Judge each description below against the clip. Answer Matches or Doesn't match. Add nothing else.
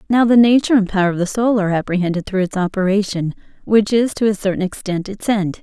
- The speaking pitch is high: Matches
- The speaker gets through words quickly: Matches